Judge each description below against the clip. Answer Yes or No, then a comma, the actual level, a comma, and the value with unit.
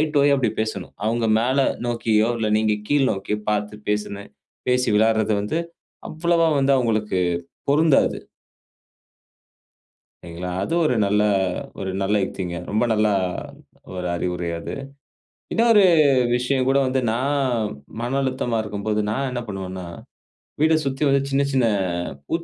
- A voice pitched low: Yes, low, 115 Hz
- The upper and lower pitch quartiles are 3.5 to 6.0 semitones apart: Yes, average, 4.5 semitones